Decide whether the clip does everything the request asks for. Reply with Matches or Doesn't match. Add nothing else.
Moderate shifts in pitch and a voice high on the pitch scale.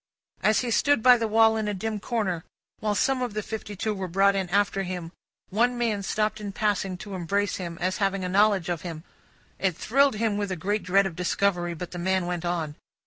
Matches